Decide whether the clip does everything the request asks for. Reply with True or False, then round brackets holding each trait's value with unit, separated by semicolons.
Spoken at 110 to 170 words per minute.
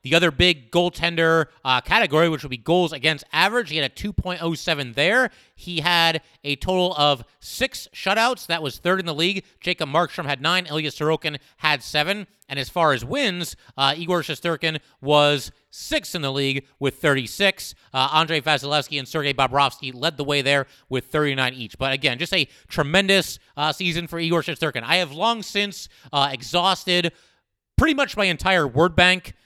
False (180 wpm)